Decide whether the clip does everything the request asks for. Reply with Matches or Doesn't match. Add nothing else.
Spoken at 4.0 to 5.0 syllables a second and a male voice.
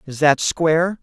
Matches